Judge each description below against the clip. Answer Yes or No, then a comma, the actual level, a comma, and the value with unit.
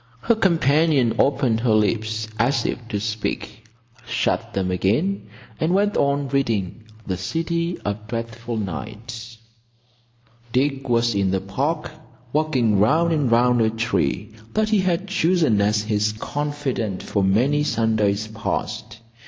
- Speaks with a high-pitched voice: No, low, 115 Hz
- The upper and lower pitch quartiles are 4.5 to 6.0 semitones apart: Yes, wide, 5.5 semitones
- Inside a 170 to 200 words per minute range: No, slow, 135 wpm